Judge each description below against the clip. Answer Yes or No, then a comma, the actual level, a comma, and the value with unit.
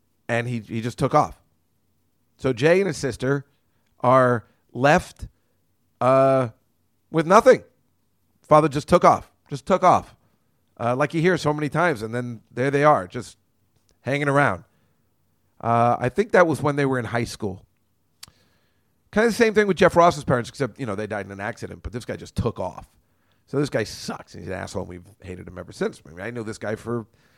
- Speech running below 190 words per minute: No, fast, 205 wpm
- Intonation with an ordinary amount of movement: No, wide, 5.7 semitones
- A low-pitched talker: Yes, low, 120 Hz